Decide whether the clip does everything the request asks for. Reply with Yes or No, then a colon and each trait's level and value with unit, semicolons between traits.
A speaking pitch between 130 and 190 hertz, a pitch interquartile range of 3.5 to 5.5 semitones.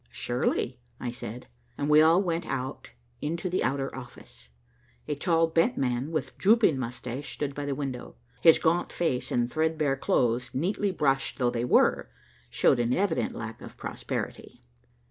Yes: medium, 140 Hz; average, 4.7 semitones